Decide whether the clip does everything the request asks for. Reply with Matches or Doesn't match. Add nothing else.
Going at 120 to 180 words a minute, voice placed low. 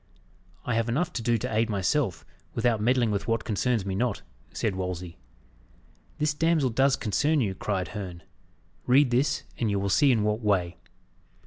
Matches